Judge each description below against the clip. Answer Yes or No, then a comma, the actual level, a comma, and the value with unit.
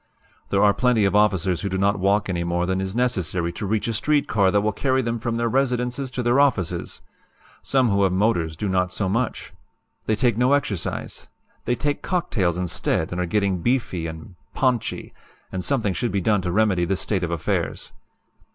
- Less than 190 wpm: No, fast, 205 wpm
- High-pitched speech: No, low, 100 Hz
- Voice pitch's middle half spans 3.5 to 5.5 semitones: Yes, average, 4.7 semitones